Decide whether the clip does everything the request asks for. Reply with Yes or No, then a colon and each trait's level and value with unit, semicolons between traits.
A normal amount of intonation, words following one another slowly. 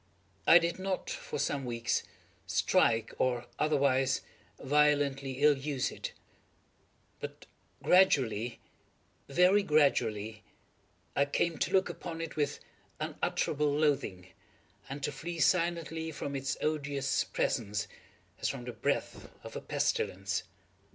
Yes: average, 4.4 semitones; slow, 110 wpm